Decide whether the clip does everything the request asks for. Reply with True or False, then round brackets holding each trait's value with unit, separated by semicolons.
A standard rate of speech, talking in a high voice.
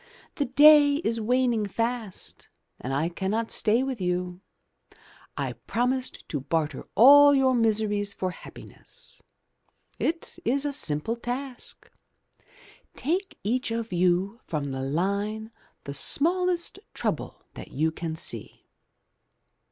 False (120 wpm; 225 Hz)